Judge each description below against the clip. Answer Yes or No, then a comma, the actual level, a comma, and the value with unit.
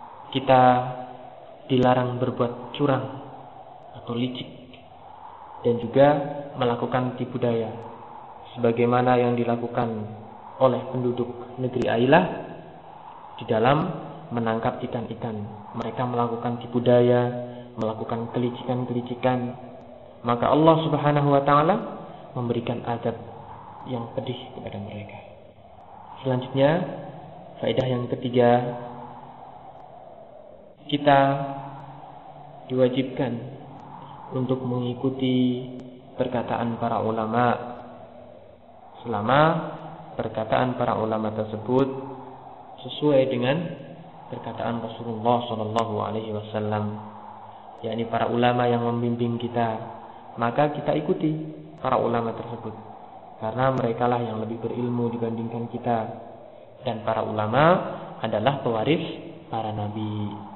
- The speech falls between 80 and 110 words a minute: Yes, slow, 85 wpm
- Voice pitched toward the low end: Yes, low, 125 Hz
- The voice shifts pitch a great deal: No, narrow, 2.4 semitones